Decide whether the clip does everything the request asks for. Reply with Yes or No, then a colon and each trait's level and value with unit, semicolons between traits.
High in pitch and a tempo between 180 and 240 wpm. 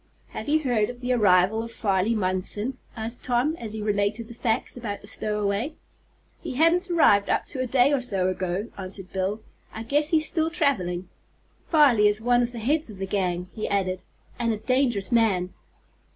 Yes: high, 220 Hz; average, 190 wpm